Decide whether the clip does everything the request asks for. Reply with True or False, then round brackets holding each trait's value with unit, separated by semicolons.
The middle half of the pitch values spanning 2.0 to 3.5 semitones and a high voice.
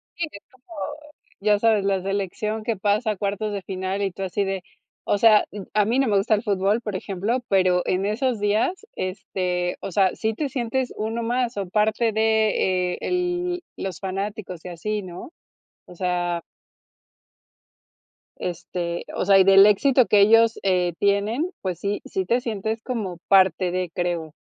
True (3.1 semitones; 200 Hz)